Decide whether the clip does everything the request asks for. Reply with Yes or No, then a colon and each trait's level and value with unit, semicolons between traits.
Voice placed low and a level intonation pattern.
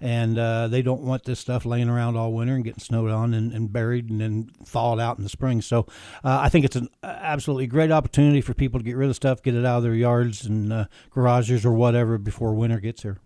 Yes: low, 120 Hz; narrow, 2.0 semitones